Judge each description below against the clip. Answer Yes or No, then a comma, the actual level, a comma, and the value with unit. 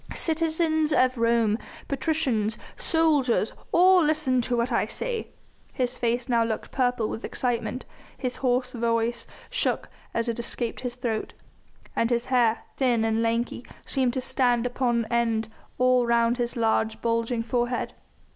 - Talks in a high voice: Yes, high, 240 Hz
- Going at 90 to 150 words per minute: Yes, average, 145 wpm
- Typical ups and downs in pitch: No, narrow, 1.9 semitones